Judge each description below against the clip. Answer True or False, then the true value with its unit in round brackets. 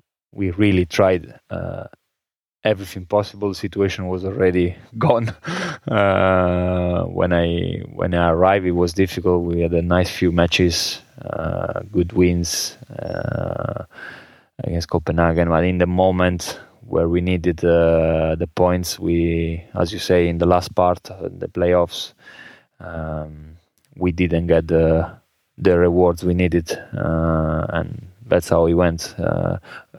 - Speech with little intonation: True (1.7 semitones)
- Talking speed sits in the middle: False (140 wpm)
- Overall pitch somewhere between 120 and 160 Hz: False (90 Hz)